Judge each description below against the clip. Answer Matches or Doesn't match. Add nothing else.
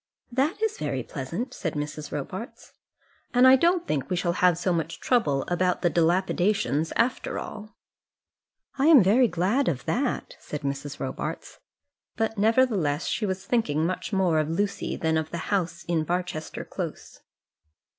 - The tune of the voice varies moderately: Doesn't match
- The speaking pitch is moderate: Matches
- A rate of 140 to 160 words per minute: Matches